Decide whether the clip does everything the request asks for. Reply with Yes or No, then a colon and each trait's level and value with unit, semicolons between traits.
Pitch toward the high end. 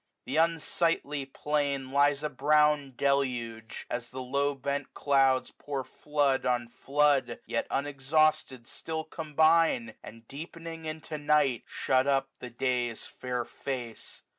No: medium, 140 Hz